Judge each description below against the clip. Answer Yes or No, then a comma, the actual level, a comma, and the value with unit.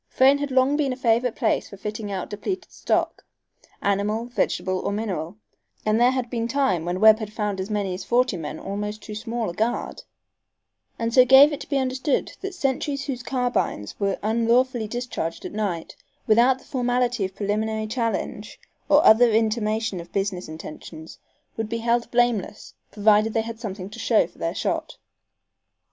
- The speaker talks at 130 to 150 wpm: No, average, 175 wpm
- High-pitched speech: Yes, high, 225 Hz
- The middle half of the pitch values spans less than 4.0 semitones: Yes, average, 3.5 semitones